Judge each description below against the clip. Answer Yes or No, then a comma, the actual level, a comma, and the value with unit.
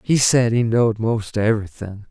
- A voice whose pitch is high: No, low, 110 Hz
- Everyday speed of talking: Yes, average, 170 wpm